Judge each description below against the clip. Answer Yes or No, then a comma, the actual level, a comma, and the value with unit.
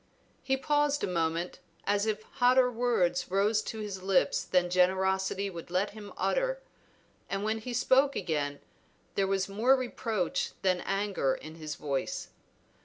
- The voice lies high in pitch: Yes, high, 195 Hz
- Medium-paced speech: Yes, average, 150 wpm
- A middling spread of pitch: Yes, average, 4.4 semitones